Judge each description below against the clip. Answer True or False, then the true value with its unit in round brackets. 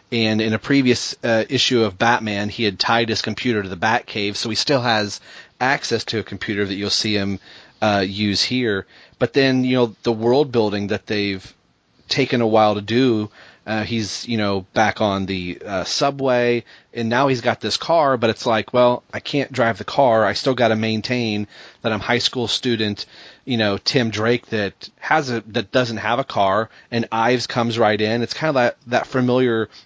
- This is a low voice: True (115 Hz)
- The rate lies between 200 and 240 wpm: True (205 wpm)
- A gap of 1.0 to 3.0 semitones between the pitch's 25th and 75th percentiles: True (2.7 semitones)